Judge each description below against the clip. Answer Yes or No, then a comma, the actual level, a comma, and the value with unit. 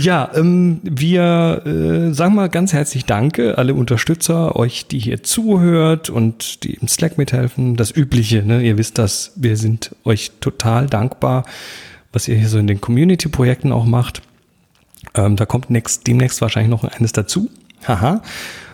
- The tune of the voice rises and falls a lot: Yes, wide, 6.0 semitones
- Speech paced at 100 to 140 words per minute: No, average, 165 wpm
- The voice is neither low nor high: No, low, 125 Hz